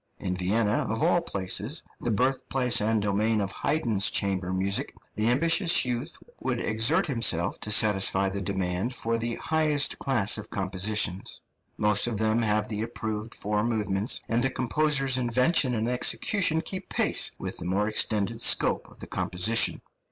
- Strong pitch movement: No, average, 4.0 semitones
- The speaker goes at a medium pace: Yes, average, 160 wpm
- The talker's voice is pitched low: Yes, low, 110 Hz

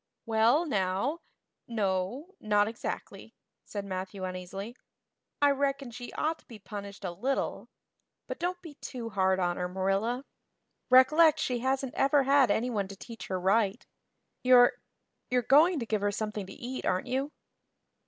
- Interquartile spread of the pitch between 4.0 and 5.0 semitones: No, wide, 5.6 semitones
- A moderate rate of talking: Yes, average, 155 wpm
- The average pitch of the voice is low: No, high, 230 Hz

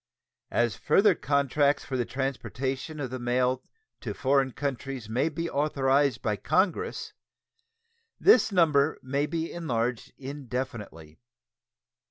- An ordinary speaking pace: No, slow, 115 wpm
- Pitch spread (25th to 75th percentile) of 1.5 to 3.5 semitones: Yes, average, 2.9 semitones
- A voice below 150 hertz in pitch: Yes, low, 135 Hz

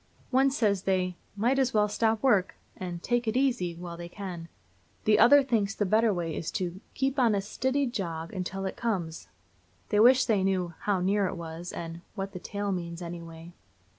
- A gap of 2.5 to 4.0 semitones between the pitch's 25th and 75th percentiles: No, average, 4.6 semitones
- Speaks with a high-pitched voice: Yes, high, 195 Hz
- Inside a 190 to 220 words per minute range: Yes, average, 195 wpm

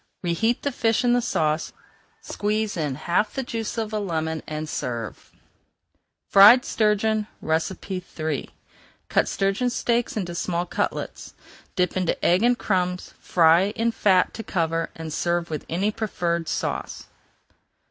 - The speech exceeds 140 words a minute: No, slow, 135 wpm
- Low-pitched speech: No, medium, 185 Hz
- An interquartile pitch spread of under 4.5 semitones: No, average, 4.8 semitones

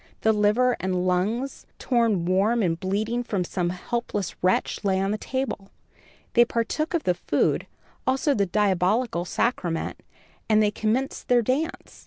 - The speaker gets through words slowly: No, average, 150 wpm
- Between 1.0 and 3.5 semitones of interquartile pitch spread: No, average, 4.4 semitones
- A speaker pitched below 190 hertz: No, high, 210 Hz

